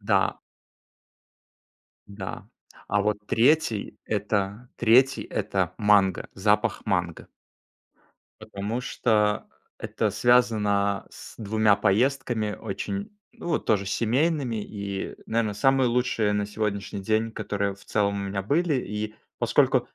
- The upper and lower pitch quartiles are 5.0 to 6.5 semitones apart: No, average, 3.0 semitones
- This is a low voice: Yes, low, 105 Hz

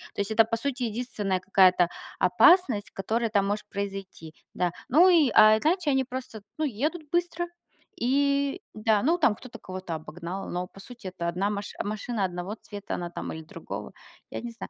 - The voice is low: No, high, 215 Hz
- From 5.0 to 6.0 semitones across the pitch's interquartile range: Yes, wide, 5.5 semitones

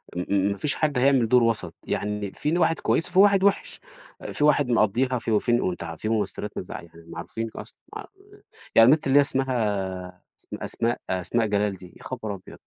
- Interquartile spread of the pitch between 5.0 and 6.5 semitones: Yes, wide, 5.4 semitones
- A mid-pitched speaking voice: No, low, 115 Hz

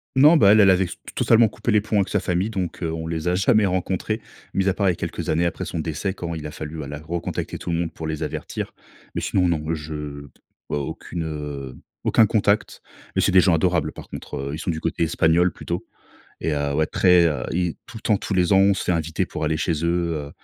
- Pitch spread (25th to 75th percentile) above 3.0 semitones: Yes, average, 3.5 semitones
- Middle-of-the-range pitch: No, very low, 85 Hz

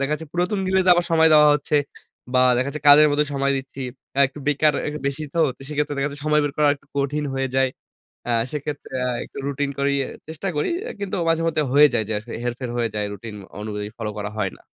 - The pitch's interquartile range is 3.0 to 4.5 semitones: No, narrow, 2.4 semitones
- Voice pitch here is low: No, medium, 145 Hz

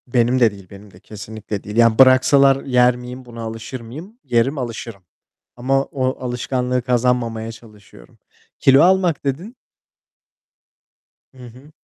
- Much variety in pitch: No, average, 2.8 semitones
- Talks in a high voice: No, low, 125 Hz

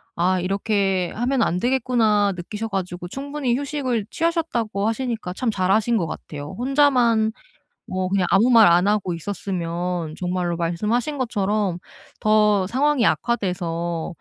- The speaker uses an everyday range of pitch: Yes, average, 4.9 semitones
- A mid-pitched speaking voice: No, high, 205 Hz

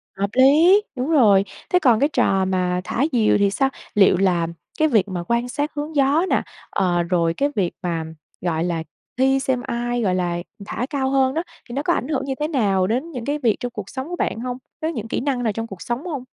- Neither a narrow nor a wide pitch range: No, wide, 6.2 semitones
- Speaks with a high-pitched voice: Yes, high, 240 Hz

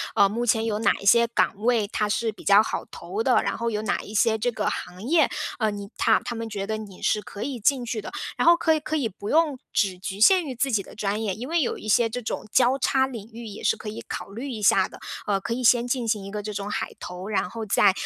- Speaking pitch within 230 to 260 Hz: No, high, 220 Hz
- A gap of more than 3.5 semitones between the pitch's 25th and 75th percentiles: No, average, 3.0 semitones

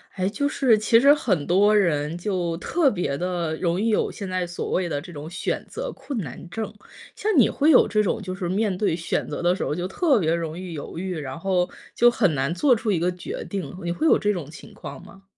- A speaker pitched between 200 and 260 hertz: No, medium, 185 Hz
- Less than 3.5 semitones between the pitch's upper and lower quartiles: No, average, 4.0 semitones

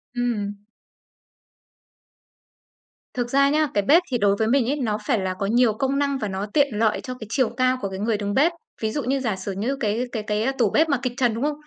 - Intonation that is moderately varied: Yes, average, 4.5 semitones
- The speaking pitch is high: Yes, high, 240 Hz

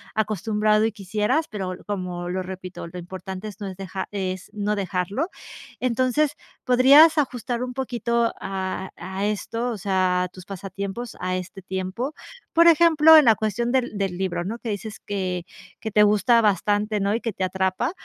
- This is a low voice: No, high, 205 Hz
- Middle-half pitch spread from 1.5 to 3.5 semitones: No, average, 4.0 semitones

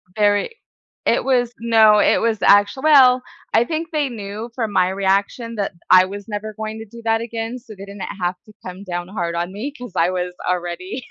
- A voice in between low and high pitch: No, high, 210 Hz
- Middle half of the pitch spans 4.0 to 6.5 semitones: No, average, 3.5 semitones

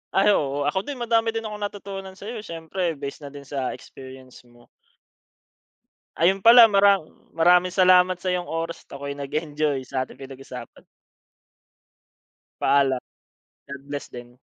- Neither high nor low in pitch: Yes, medium, 165 Hz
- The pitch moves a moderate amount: No, wide, 6.0 semitones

